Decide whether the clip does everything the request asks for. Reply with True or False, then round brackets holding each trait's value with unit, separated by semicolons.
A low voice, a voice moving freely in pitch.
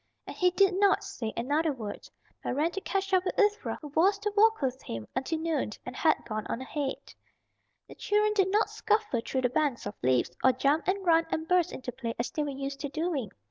False (310 Hz; 6.7 semitones)